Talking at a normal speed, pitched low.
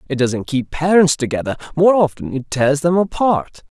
No: average, 175 wpm; medium, 150 Hz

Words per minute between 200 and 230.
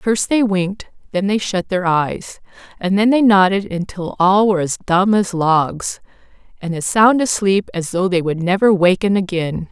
No: average, 185 wpm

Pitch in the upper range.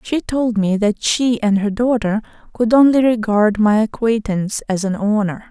Yes: high, 220 Hz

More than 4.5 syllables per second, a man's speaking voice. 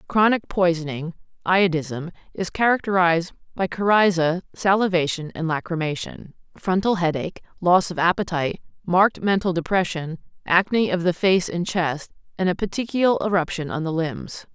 No: 5.1 syllables/s; female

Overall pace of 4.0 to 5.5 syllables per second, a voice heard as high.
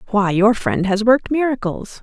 Yes: 5.0 syllables/s; high, 215 Hz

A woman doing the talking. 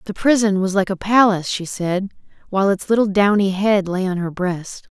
Yes: female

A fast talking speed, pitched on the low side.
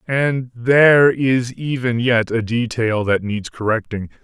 No: average, 140 wpm; low, 120 Hz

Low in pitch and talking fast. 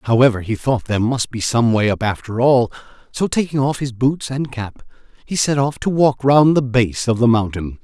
Yes: low, 125 Hz; fast, 220 wpm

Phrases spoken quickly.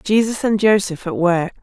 No: average, 185 wpm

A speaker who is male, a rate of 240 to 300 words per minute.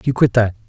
Yes: male; fast, 265 wpm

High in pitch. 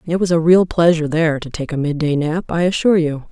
No: medium, 160 Hz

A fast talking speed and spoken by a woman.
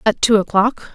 No: average, 190 wpm; female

